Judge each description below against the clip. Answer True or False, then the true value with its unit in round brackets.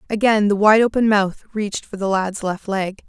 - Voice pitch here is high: True (205 Hz)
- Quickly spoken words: True (215 wpm)